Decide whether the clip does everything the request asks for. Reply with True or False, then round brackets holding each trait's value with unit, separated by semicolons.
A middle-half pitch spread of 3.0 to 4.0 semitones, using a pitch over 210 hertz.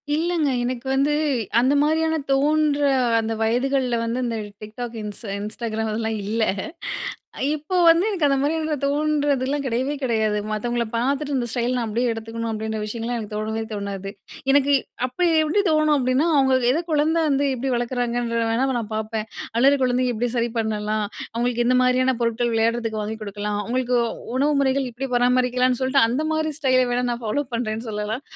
True (3.7 semitones; 245 Hz)